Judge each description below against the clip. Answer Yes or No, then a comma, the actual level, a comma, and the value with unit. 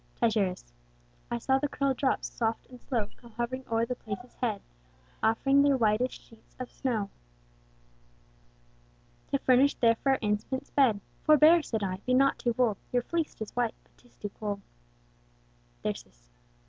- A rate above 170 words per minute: No, average, 155 wpm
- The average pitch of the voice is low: No, high, 240 Hz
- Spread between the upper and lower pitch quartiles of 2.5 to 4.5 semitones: Yes, average, 3.7 semitones